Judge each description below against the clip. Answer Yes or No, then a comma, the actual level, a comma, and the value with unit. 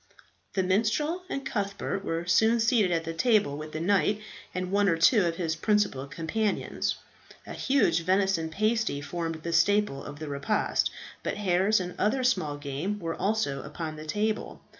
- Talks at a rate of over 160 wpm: Yes, average, 170 wpm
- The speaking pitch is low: No, medium, 185 Hz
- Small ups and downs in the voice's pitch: No, average, 4.6 semitones